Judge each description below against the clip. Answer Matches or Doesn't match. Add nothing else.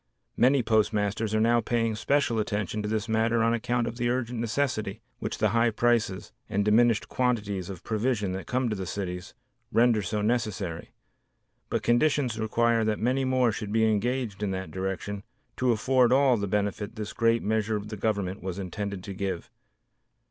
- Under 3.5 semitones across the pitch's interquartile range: Matches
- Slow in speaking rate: Doesn't match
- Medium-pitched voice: Doesn't match